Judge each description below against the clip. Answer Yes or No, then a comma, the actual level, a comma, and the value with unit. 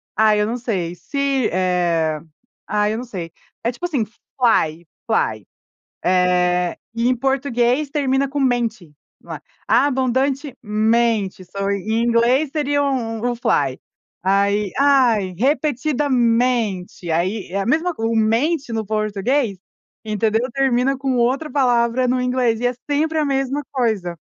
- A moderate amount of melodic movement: Yes, average, 4.8 semitones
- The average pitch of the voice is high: Yes, high, 235 Hz